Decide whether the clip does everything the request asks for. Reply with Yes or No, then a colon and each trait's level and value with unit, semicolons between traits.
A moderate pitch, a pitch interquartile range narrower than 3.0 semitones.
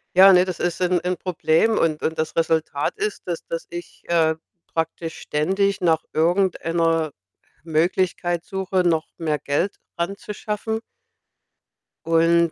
Yes: medium, 170 Hz; narrow, 2.4 semitones